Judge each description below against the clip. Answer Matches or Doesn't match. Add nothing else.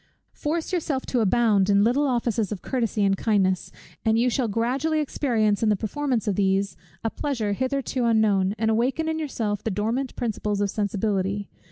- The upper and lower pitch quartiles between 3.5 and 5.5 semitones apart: Matches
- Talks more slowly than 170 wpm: Doesn't match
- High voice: Matches